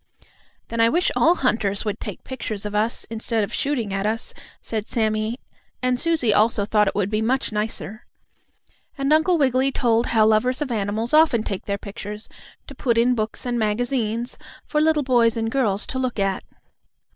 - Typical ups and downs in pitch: Yes, average, 3.3 semitones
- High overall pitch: Yes, high, 230 Hz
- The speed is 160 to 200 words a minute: Yes, average, 180 wpm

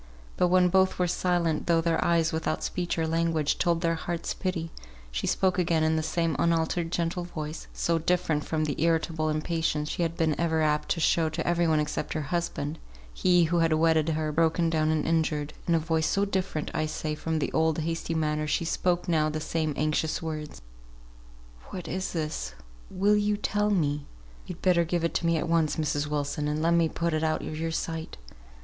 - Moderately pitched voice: Yes, medium, 165 Hz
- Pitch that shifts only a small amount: Yes, narrow, 1.6 semitones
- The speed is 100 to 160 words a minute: No, fast, 205 wpm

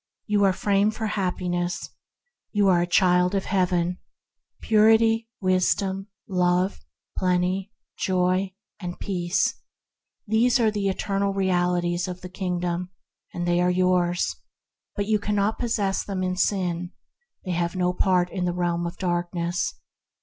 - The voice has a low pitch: No, medium, 185 Hz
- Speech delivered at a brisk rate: No, average, 140 wpm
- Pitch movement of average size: No, narrow, 2.0 semitones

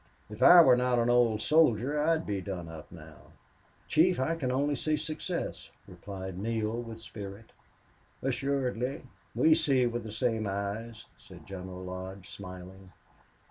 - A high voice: No, low, 115 Hz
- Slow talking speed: No, average, 150 wpm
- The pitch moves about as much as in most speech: No, wide, 5.9 semitones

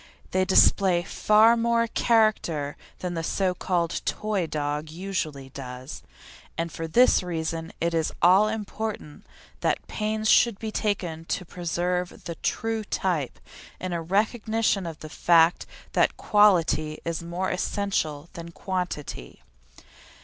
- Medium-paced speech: No, slow, 130 wpm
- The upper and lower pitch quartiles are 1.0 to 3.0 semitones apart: No, average, 4.3 semitones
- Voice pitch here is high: No, medium, 180 Hz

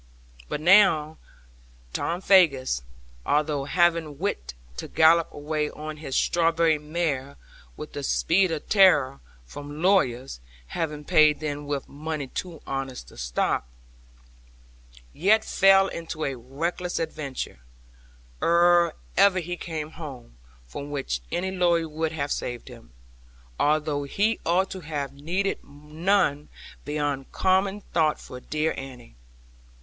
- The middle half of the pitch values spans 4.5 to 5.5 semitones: No, average, 3.4 semitones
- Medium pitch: Yes, medium, 155 Hz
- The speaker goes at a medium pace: No, slow, 125 wpm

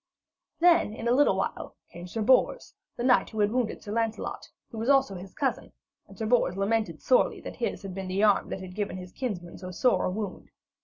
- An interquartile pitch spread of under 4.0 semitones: No, average, 4.6 semitones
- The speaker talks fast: Yes, fast, 220 wpm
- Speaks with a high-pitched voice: Yes, high, 215 Hz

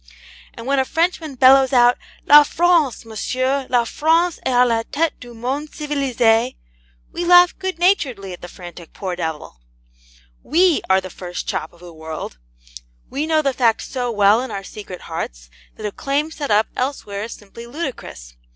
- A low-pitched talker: No, very high, 250 Hz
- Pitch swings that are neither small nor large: No, wide, 6.8 semitones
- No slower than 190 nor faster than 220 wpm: No, average, 175 wpm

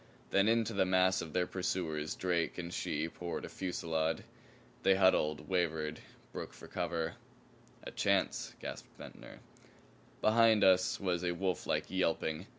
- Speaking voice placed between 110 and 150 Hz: No, very low, 90 Hz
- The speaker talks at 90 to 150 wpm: Yes, average, 140 wpm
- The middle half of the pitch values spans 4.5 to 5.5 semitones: No, narrow, 2.6 semitones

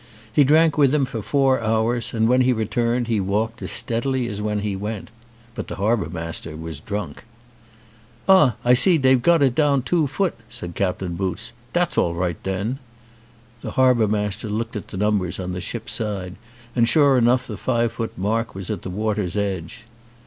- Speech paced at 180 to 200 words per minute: Yes, average, 190 wpm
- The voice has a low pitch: Yes, low, 110 Hz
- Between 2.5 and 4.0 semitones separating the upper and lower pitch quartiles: No, average, 4.5 semitones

